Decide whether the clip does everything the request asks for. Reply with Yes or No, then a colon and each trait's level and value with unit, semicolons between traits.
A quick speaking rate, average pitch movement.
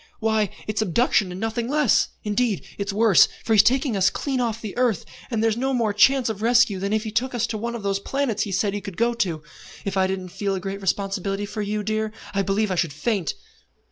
Yes: fast, 235 wpm; average, 3.0 semitones